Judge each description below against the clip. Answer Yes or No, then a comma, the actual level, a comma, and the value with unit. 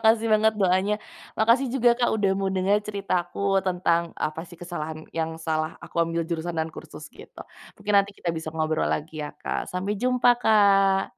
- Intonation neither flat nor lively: Yes, average, 4.2 semitones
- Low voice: No, medium, 185 Hz